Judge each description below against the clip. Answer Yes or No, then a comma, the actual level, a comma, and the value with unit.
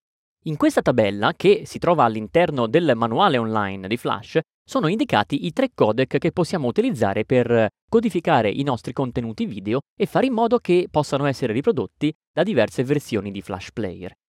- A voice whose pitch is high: No, medium, 140 Hz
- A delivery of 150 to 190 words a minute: Yes, fast, 170 wpm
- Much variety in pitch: Yes, wide, 8.2 semitones